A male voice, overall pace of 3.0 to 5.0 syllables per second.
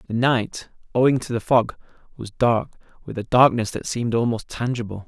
No: male; 5.4 syllables/s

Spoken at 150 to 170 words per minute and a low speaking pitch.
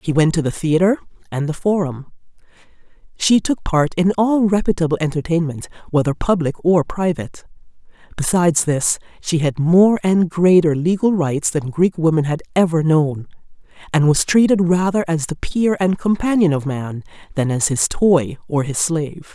No: average, 160 wpm; medium, 165 Hz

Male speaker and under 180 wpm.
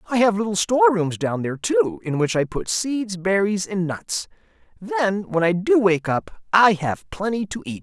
No: male; average, 200 wpm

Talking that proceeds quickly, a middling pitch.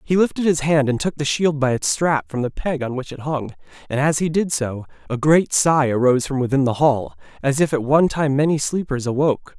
Yes: fast, 245 wpm; medium, 145 Hz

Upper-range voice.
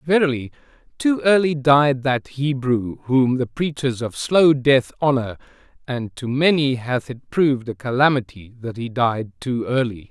No: low, 130 Hz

